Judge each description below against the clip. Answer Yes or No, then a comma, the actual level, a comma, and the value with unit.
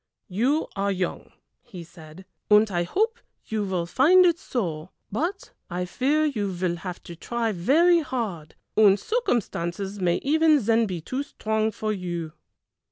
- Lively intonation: Yes, wide, 7.2 semitones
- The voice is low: No, high, 210 Hz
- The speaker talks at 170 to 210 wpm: No, average, 155 wpm